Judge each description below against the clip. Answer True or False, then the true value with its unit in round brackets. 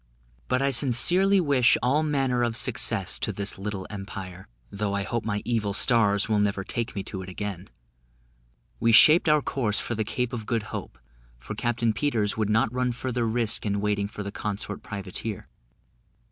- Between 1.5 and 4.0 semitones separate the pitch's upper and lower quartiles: True (3.3 semitones)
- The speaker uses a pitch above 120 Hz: False (110 Hz)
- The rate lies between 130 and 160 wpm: False (180 wpm)